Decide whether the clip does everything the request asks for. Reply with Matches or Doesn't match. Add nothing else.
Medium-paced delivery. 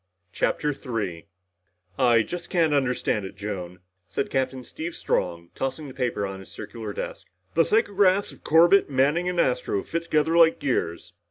Matches